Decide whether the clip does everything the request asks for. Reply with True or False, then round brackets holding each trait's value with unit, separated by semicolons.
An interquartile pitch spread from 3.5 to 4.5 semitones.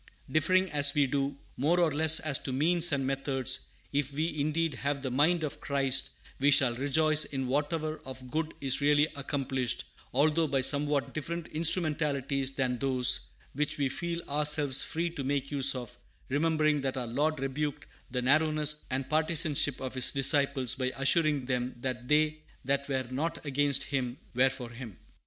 False (2.6 semitones)